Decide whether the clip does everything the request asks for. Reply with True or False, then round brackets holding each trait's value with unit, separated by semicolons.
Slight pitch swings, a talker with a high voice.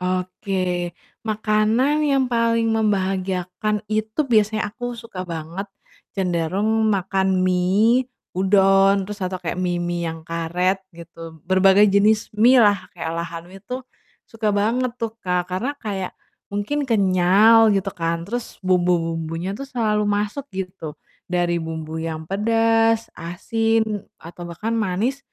False (3.8 semitones; 195 Hz)